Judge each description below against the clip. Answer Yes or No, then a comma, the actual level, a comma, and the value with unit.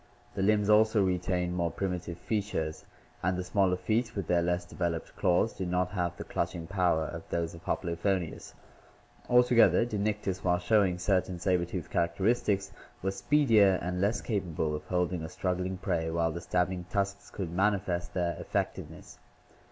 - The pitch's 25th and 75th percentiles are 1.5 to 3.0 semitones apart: Yes, narrow, 2.4 semitones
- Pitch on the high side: No, very low, 90 Hz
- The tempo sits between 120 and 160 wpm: Yes, average, 155 wpm